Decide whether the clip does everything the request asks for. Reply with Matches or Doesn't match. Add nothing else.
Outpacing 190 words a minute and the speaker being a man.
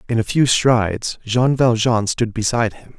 Doesn't match